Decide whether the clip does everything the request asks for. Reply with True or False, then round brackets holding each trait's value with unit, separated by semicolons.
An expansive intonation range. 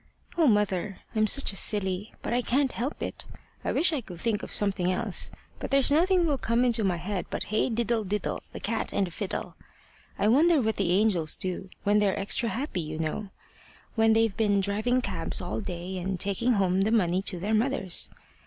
False (3.8 semitones)